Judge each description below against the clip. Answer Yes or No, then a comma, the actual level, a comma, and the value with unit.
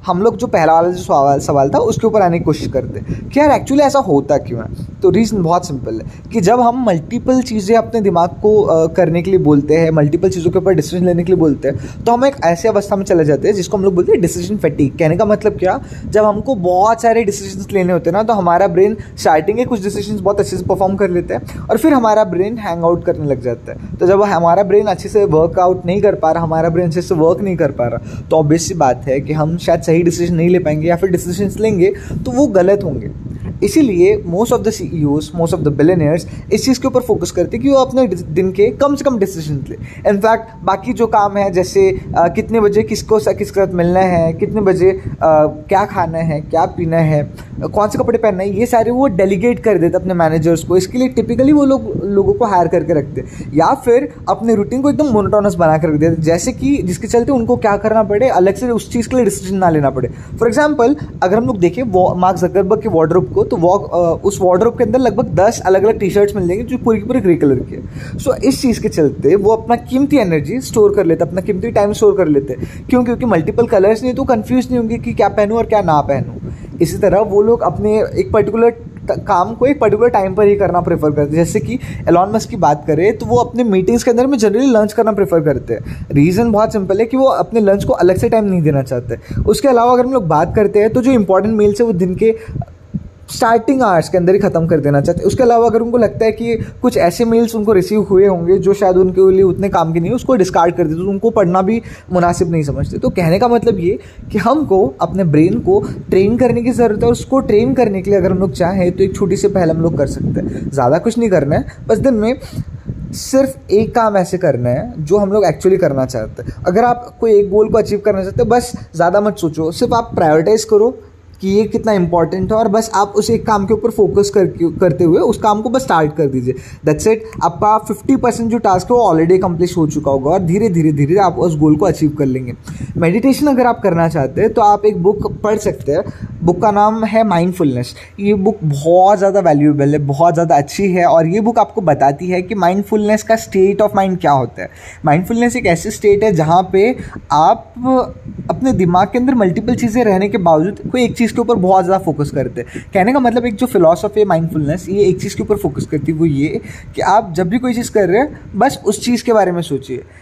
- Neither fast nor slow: No, fast, 245 wpm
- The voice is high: Yes, high, 195 Hz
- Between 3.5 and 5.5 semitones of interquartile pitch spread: Yes, average, 5.1 semitones